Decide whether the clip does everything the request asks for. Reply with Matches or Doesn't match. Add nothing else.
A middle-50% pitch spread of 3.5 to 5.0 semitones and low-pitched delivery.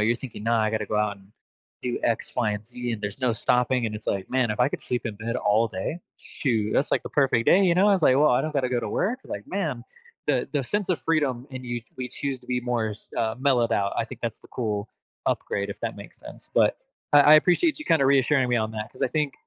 Matches